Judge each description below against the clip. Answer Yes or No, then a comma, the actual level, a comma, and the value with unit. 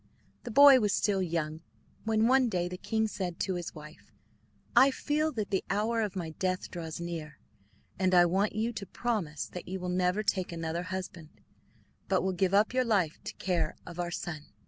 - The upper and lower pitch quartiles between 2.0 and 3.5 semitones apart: No, average, 3.9 semitones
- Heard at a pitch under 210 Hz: Yes, medium, 185 Hz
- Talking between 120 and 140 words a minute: No, average, 200 wpm